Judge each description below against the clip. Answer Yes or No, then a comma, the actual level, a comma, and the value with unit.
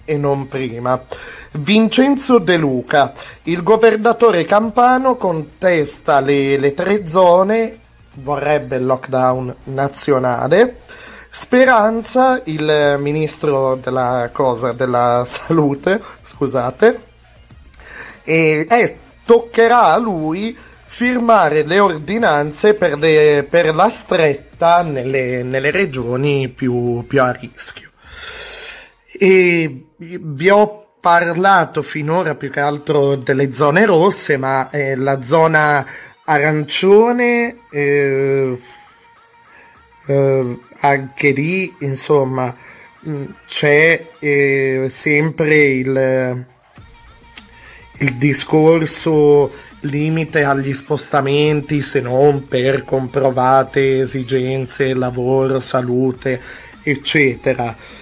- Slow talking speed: Yes, slow, 85 wpm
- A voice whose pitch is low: No, medium, 145 Hz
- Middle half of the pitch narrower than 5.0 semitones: No, average, 5.3 semitones